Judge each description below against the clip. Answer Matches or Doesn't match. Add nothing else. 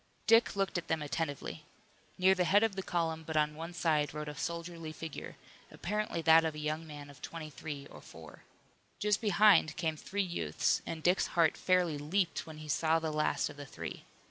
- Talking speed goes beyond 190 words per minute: Matches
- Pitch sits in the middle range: Matches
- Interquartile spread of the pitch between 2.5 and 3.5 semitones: Matches